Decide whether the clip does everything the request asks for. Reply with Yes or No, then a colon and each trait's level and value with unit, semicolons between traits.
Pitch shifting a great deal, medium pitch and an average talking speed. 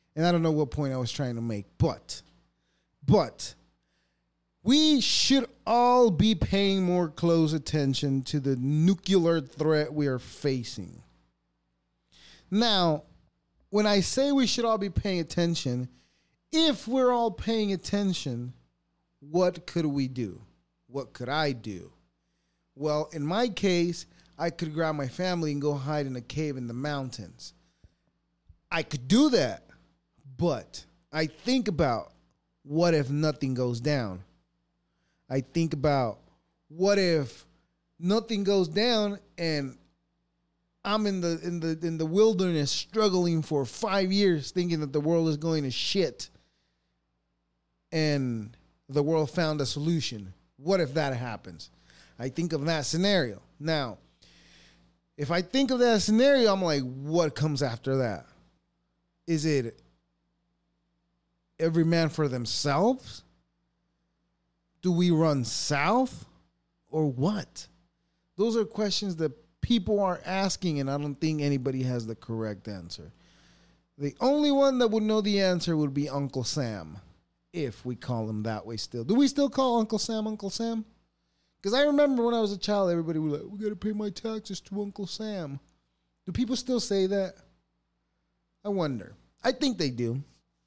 Yes: wide, 7.2 semitones; medium, 160 Hz; average, 150 wpm